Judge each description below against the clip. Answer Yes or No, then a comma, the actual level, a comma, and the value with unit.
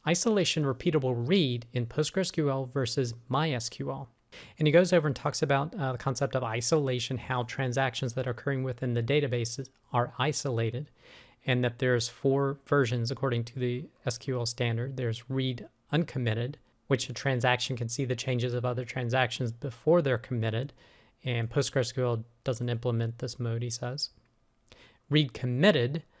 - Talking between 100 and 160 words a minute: Yes, average, 150 wpm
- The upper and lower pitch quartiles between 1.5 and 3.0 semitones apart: Yes, narrow, 2.5 semitones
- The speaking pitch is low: Yes, low, 130 Hz